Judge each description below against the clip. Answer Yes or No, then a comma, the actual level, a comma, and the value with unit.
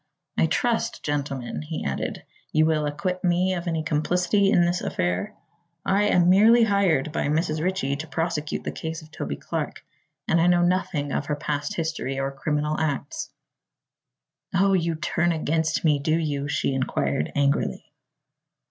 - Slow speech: No, average, 155 wpm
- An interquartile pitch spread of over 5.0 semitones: No, average, 3.5 semitones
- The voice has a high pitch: No, medium, 160 Hz